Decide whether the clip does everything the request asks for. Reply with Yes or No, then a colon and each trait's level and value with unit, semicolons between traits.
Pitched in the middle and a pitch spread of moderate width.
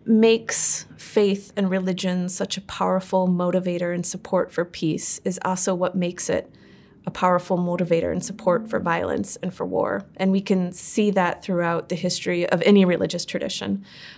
No: medium, 180 Hz; narrow, 1.7 semitones